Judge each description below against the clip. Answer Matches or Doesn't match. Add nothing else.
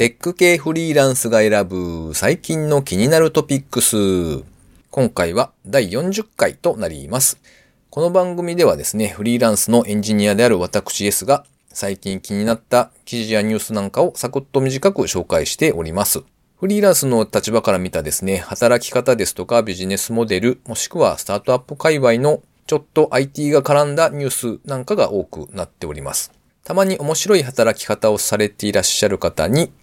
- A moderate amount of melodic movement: Doesn't match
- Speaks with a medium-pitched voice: Doesn't match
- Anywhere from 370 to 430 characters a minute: Matches